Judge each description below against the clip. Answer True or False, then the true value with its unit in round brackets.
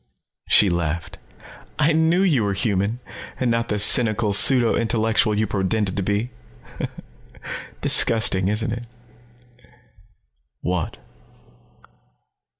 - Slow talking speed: True (100 wpm)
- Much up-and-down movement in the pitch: False (3.1 semitones)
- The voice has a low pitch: True (110 Hz)